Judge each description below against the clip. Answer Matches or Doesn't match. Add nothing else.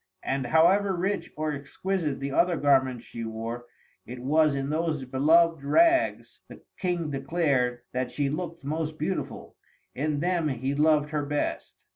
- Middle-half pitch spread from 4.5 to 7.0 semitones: Doesn't match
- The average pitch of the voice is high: Doesn't match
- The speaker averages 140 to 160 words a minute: Matches